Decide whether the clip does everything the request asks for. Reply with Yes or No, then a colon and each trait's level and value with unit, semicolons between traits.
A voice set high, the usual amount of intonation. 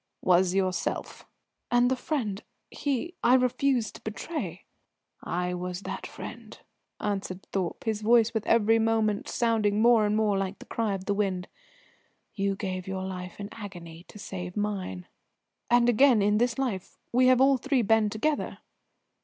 Yes: high, 210 Hz; average, 3.8 semitones